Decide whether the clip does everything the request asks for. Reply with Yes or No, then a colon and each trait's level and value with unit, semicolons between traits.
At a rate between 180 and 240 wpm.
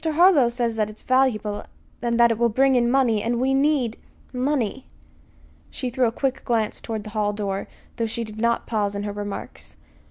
Yes: average, 200 wpm